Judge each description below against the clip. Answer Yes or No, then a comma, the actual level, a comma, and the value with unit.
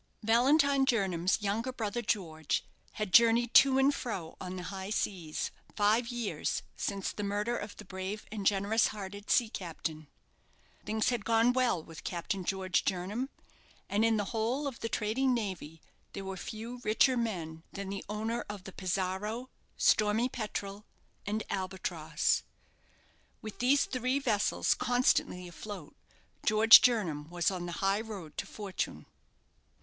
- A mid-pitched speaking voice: No, high, 210 Hz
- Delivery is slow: No, average, 145 wpm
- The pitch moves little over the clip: No, average, 3.8 semitones